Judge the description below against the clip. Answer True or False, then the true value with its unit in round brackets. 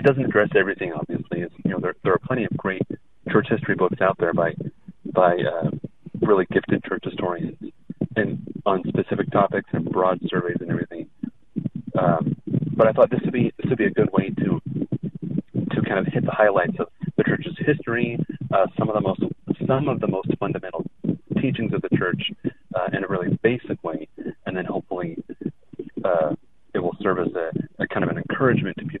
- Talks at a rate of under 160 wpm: False (195 wpm)